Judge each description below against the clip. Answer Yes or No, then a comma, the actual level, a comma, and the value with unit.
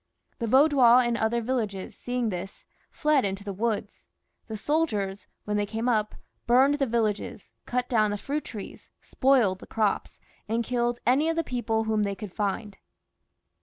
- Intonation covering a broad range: No, average, 3.3 semitones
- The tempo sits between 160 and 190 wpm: Yes, average, 170 wpm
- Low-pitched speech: No, high, 225 Hz